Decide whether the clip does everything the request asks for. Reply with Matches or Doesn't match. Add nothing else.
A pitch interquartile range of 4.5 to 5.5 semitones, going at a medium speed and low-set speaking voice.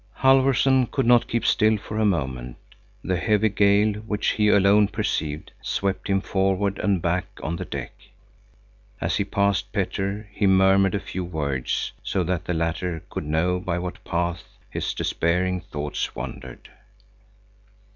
Doesn't match